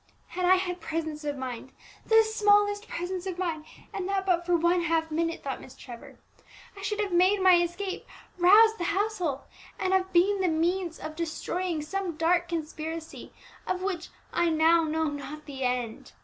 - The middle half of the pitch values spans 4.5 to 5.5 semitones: No, average, 3.2 semitones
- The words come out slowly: No, average, 175 wpm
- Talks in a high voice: Yes, very high, 345 Hz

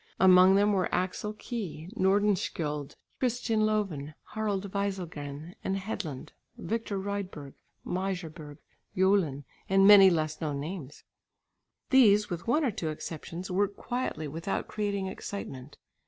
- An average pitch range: Yes, average, 4.5 semitones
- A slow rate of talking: Yes, slow, 115 wpm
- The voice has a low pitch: No, high, 190 Hz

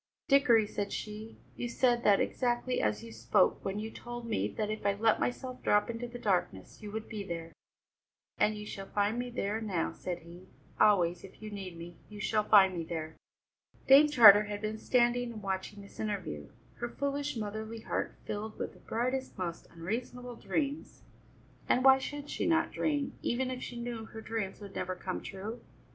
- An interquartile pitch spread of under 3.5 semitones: No, average, 3.8 semitones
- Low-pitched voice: No, high, 215 Hz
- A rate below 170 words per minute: No, average, 190 wpm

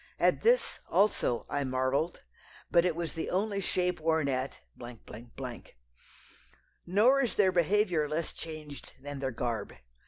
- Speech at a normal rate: No, slow, 130 wpm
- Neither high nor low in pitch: Yes, medium, 165 Hz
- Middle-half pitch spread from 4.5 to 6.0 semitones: Yes, average, 5.2 semitones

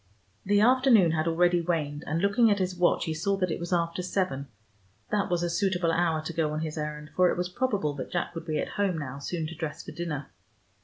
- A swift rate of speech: Yes, fast, 240 wpm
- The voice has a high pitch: No, medium, 170 Hz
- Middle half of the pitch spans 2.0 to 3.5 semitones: Yes, average, 2.9 semitones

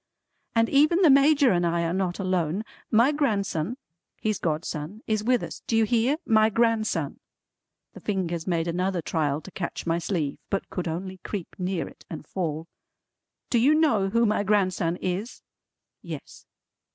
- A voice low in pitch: No, high, 195 Hz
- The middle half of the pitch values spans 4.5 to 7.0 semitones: Yes, average, 4.9 semitones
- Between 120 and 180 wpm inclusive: Yes, average, 165 wpm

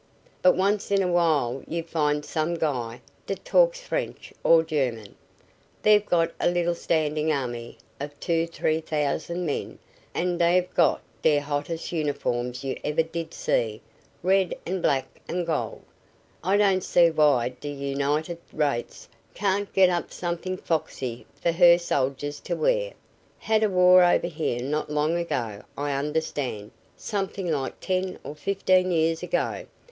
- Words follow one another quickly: No, average, 150 wpm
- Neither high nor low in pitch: Yes, medium, 165 Hz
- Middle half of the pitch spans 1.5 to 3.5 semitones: No, average, 3.9 semitones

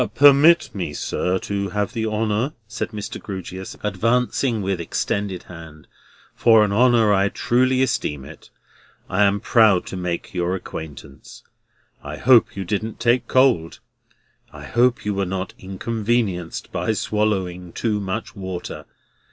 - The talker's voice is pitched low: Yes, low, 100 Hz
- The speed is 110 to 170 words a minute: Yes, average, 140 wpm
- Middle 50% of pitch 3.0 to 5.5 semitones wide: Yes, average, 4.0 semitones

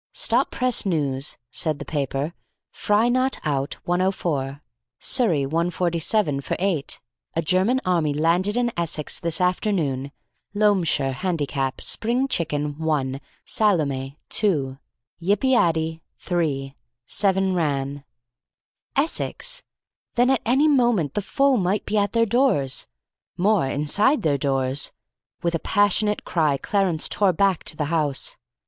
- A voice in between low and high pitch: Yes, medium, 170 Hz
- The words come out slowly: Yes, slow, 130 wpm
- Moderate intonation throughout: No, wide, 6.3 semitones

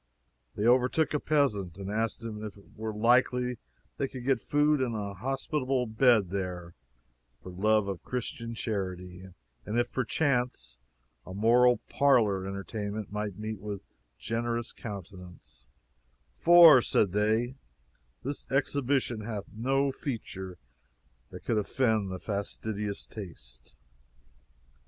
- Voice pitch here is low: Yes, low, 110 Hz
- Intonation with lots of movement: No, average, 4.0 semitones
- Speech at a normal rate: No, slow, 125 wpm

